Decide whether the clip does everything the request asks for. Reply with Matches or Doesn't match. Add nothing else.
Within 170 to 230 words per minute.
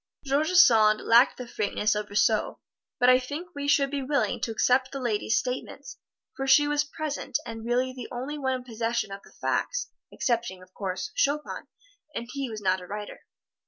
Matches